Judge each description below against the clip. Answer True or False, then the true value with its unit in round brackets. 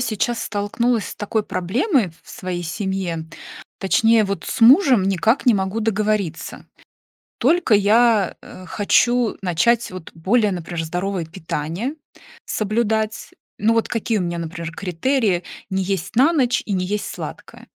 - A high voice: True (205 Hz)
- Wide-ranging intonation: False (4.1 semitones)